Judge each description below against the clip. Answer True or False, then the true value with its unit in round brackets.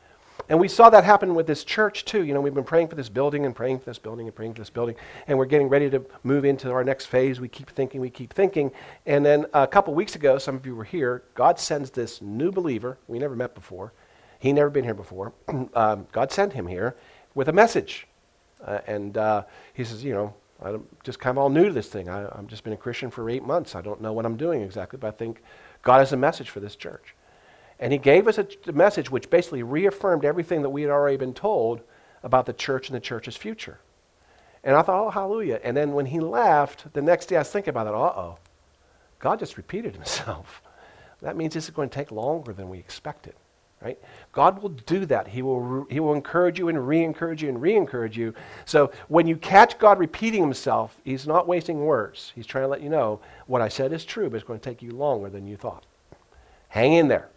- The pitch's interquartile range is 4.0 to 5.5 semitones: True (5.1 semitones)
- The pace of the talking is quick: True (240 wpm)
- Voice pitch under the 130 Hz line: False (135 Hz)